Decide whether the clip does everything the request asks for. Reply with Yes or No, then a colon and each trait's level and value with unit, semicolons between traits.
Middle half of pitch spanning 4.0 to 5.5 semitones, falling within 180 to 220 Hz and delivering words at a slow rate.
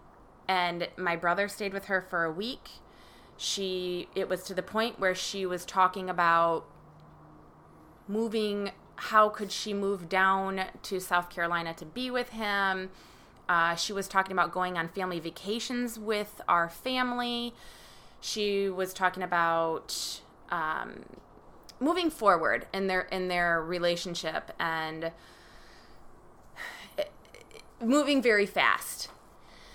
No: average, 3.1 semitones; high, 190 Hz; slow, 125 wpm